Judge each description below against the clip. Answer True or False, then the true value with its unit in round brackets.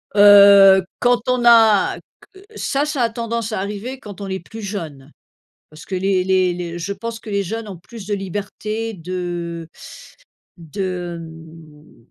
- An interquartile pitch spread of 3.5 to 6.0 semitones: True (4.3 semitones)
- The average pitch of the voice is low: False (195 Hz)